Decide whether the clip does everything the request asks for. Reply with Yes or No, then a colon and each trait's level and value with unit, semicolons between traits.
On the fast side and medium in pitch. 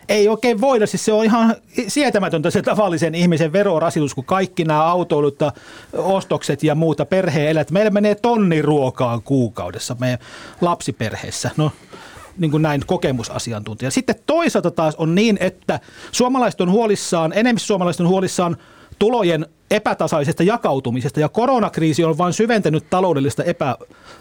No: average, 140 wpm; medium, 170 Hz